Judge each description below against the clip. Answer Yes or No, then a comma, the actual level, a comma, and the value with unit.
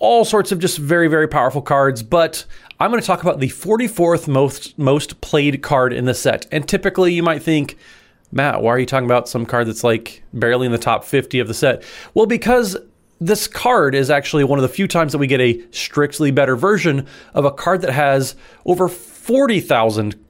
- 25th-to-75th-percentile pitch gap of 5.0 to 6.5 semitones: Yes, wide, 5.5 semitones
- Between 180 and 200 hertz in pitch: No, medium, 145 Hz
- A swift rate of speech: Yes, fast, 215 wpm